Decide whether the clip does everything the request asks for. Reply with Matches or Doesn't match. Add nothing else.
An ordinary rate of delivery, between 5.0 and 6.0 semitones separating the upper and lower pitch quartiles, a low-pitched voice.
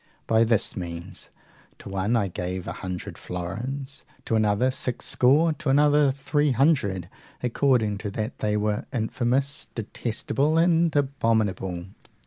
Doesn't match